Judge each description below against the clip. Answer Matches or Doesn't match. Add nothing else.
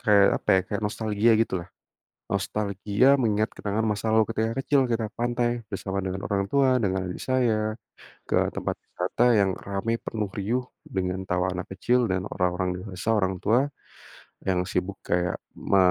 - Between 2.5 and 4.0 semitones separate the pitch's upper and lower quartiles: Matches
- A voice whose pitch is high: Doesn't match